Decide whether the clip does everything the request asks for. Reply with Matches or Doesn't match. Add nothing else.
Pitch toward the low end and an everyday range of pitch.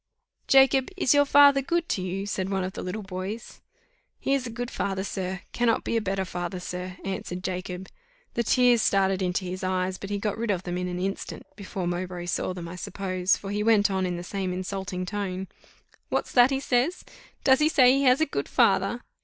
Doesn't match